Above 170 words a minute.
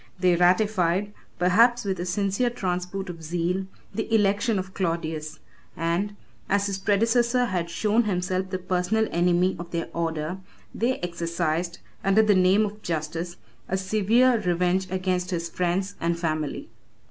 No: average, 145 wpm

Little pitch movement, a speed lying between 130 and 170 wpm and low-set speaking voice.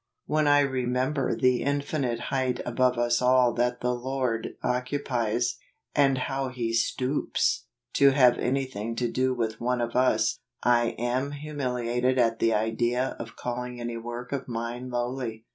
Yes: narrow, 1.7 semitones; average, 150 wpm; low, 125 Hz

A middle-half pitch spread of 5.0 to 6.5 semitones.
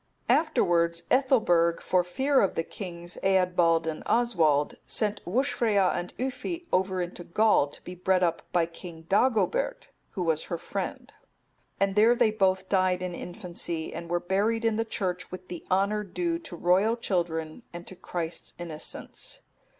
No: average, 4.1 semitones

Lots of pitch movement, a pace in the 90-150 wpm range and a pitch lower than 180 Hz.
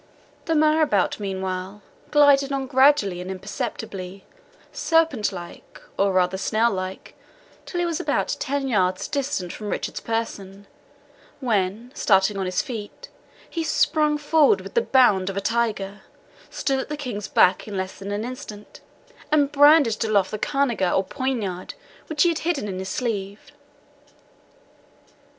No: wide, 6.7 semitones; average, 145 wpm; high, 215 Hz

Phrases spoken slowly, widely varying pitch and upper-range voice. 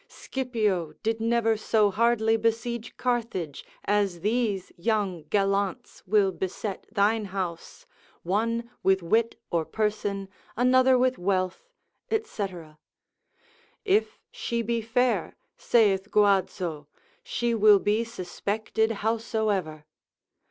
No: slow, 100 wpm; average, 3.2 semitones; high, 215 Hz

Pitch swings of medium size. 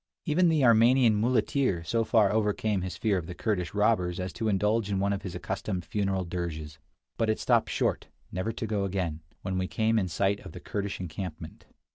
Yes: average, 3.3 semitones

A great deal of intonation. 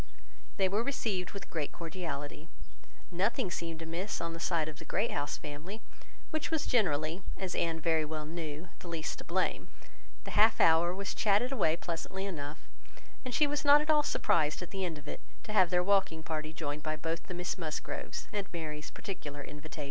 No: average, 4.1 semitones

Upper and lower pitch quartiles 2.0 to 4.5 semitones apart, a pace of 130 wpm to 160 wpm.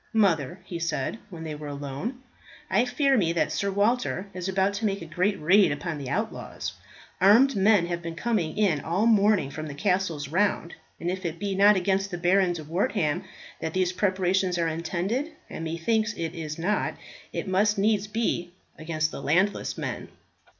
No: average, 3.9 semitones; average, 185 wpm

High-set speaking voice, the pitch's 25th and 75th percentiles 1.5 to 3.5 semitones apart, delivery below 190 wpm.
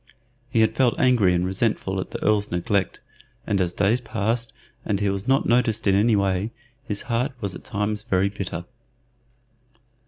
No: low, 105 Hz; average, 3.0 semitones; average, 175 wpm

